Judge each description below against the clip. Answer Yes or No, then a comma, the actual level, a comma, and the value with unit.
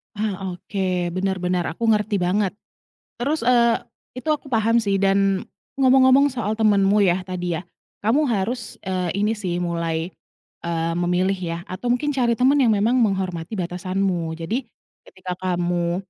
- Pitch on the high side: Yes, high, 195 Hz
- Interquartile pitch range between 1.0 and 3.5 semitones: No, average, 4.3 semitones